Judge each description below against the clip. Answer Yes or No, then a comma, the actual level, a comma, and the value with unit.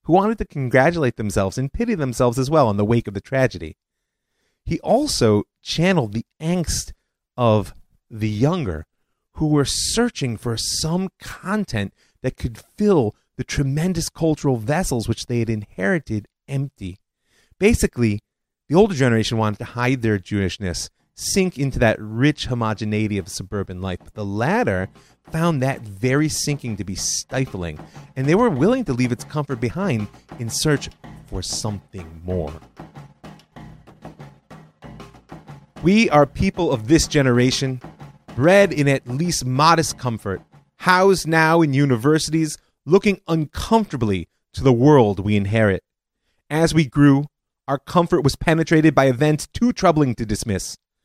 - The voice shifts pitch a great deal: Yes, wide, 6.9 semitones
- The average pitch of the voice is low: Yes, low, 130 Hz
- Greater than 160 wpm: No, average, 140 wpm